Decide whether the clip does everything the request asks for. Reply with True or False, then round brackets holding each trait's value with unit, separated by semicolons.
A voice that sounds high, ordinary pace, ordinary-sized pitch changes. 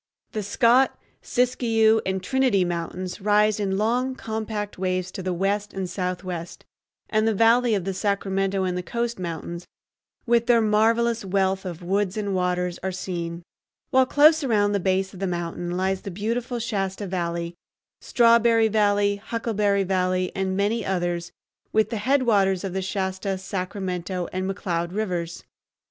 True (195 Hz; 155 wpm; 3.2 semitones)